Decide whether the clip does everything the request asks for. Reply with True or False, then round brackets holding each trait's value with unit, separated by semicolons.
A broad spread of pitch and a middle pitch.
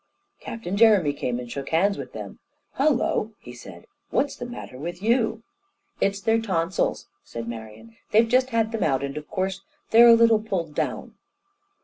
False (7.5 semitones; 200 Hz)